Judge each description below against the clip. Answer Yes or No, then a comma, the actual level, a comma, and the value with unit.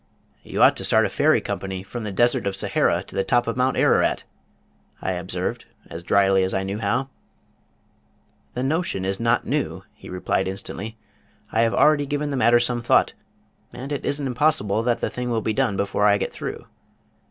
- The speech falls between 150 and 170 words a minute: No, average, 195 wpm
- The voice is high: No, low, 115 Hz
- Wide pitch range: No, average, 4.6 semitones